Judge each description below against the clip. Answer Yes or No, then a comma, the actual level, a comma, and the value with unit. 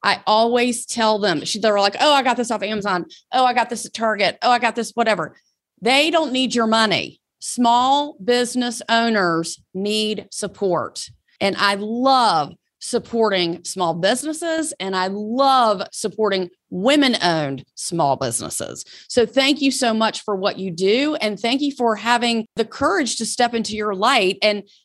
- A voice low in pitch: No, high, 220 Hz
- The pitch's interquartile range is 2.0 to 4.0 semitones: Yes, average, 3.4 semitones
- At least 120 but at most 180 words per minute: Yes, average, 165 wpm